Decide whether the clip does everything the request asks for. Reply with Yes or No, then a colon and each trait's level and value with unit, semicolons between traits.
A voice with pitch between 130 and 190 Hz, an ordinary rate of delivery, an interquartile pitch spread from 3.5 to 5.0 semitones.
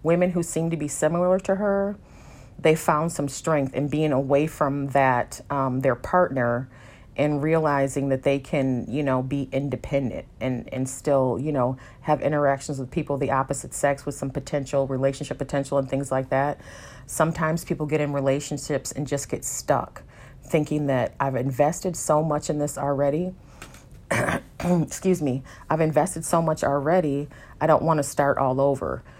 No: medium, 140 Hz; average, 170 wpm; narrow, 2.4 semitones